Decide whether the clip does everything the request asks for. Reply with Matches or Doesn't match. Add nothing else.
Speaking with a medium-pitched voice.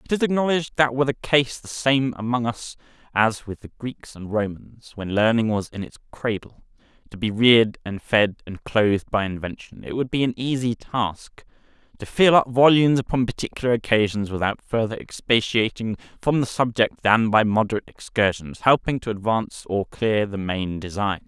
Doesn't match